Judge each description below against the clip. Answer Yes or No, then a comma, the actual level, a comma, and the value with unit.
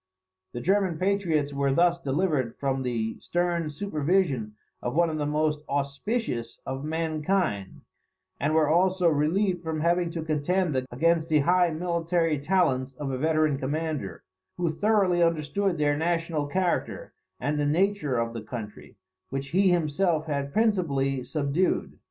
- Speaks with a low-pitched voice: No, medium, 155 Hz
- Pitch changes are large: No, average, 4.0 semitones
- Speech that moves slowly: No, average, 145 wpm